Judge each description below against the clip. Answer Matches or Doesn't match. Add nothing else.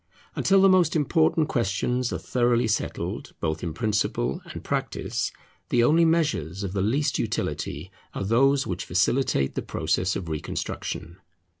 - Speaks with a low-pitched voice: Matches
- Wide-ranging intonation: Matches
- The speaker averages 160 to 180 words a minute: Doesn't match